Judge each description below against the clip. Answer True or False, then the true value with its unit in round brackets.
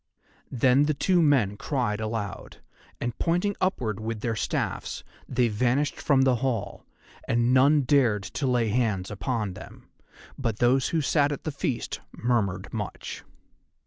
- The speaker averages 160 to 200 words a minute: False (145 wpm)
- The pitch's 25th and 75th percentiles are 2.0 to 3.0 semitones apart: False (4.3 semitones)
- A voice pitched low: True (120 Hz)